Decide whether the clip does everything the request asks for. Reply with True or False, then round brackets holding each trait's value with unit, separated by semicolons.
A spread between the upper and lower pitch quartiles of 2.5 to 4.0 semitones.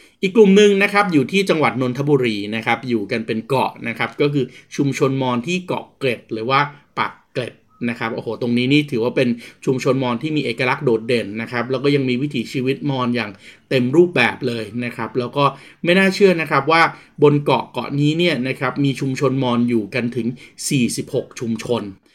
True (3.4 semitones)